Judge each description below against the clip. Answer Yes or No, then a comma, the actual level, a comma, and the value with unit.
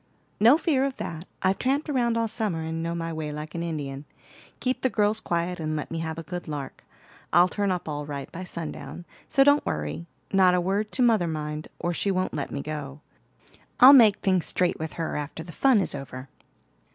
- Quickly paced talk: Yes, fast, 210 wpm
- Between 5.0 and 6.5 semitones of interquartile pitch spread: Yes, wide, 5.4 semitones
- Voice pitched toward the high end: No, medium, 170 Hz